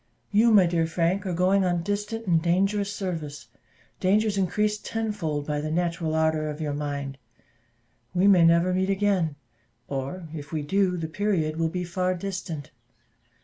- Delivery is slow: No, average, 160 wpm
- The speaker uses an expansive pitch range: No, average, 3.8 semitones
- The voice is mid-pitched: Yes, medium, 175 Hz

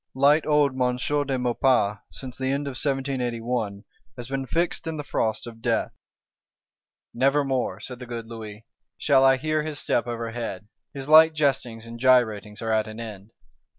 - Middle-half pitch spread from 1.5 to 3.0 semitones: No, average, 3.4 semitones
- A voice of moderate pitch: No, low, 125 Hz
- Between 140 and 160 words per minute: No, average, 170 wpm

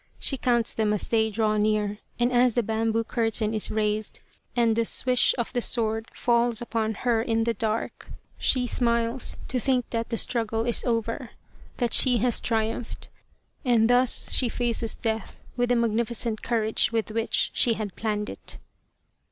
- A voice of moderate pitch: No, high, 230 Hz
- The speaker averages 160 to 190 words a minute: Yes, average, 170 wpm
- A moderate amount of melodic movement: No, narrow, 1.6 semitones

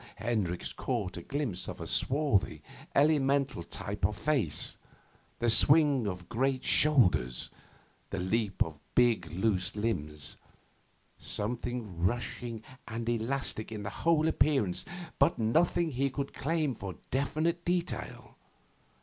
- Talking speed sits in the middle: No, slow, 120 wpm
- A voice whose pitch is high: No, low, 120 Hz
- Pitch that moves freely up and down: Yes, wide, 6.2 semitones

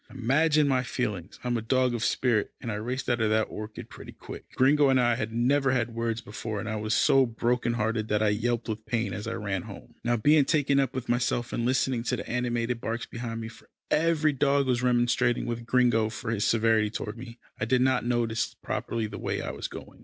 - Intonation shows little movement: Yes, narrow, 2.3 semitones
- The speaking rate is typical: No, fast, 235 wpm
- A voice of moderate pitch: No, low, 120 Hz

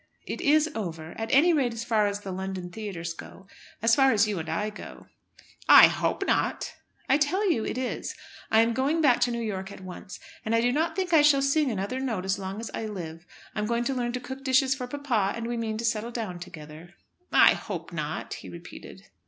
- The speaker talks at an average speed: No, fast, 225 wpm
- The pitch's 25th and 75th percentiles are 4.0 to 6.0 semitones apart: Yes, wide, 5.4 semitones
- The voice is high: Yes, high, 230 Hz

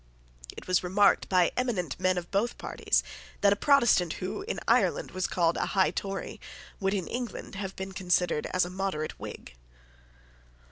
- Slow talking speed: No, average, 170 wpm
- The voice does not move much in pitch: Yes, narrow, 2.2 semitones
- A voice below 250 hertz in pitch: Yes, high, 190 Hz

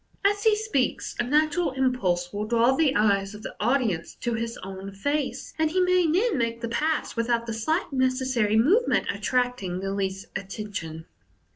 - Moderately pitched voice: No, high, 240 Hz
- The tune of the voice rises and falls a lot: Yes, wide, 6.5 semitones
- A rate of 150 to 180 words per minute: Yes, average, 175 wpm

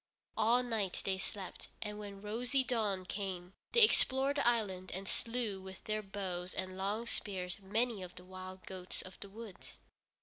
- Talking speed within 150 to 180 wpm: Yes, average, 170 wpm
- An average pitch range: Yes, average, 3.4 semitones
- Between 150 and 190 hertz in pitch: No, high, 200 Hz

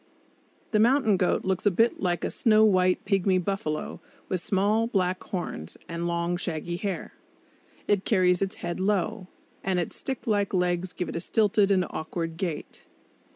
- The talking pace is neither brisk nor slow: Yes, average, 165 wpm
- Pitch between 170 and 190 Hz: Yes, medium, 185 Hz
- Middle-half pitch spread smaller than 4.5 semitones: Yes, average, 2.8 semitones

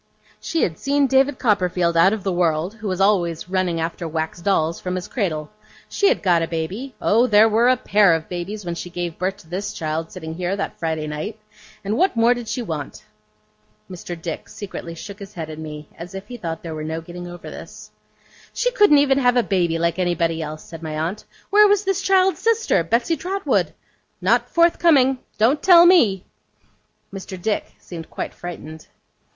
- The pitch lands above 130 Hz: Yes, medium, 185 Hz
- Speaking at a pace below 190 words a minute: No, average, 195 wpm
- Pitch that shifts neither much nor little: No, wide, 6.5 semitones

